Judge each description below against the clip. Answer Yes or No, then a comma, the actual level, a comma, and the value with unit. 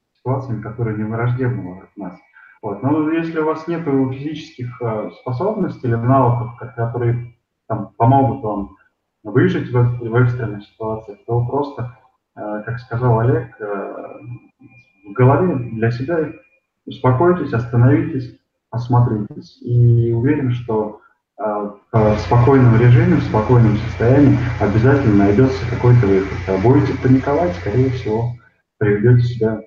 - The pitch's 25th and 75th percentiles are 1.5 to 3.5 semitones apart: Yes, average, 3.1 semitones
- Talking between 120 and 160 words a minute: No, slow, 110 wpm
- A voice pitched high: No, low, 120 Hz